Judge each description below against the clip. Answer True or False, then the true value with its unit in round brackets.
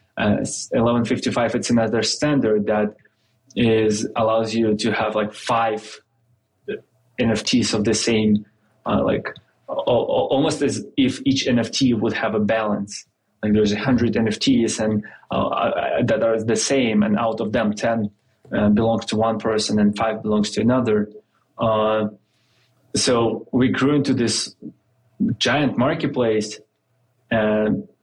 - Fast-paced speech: False (140 wpm)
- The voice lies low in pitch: True (110 Hz)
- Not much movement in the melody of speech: True (1.8 semitones)